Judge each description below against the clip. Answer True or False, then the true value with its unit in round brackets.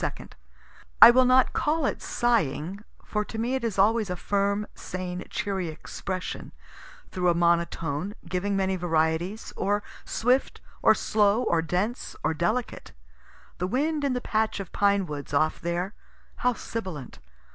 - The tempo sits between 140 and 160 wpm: True (150 wpm)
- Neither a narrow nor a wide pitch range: True (4.7 semitones)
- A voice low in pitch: False (195 Hz)